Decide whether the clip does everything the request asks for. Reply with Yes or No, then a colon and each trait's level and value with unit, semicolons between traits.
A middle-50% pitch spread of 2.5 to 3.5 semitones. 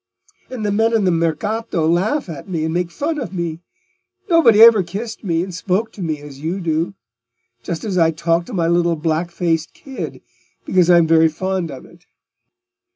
No: average, 3.9 semitones